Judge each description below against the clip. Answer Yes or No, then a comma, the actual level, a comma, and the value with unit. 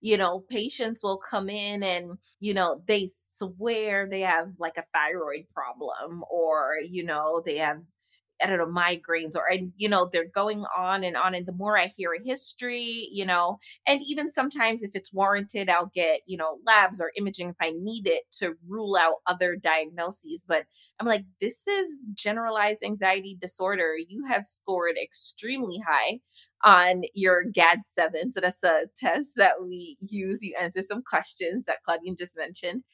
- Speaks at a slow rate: No, average, 180 wpm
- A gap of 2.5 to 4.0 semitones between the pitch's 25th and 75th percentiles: Yes, average, 3.5 semitones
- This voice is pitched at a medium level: No, high, 195 Hz